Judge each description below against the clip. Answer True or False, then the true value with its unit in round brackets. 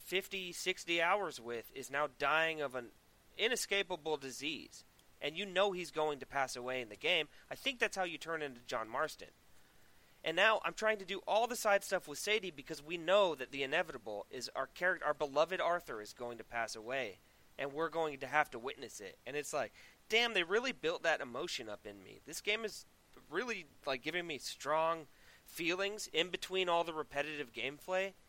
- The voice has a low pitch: False (165 Hz)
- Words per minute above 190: True (200 wpm)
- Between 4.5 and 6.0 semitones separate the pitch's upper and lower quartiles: True (5.2 semitones)